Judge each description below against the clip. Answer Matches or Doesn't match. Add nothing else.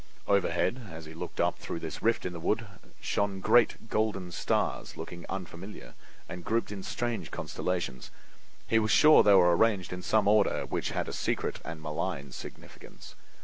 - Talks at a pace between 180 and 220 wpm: Doesn't match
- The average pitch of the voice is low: Matches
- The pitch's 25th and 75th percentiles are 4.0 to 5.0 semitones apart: Matches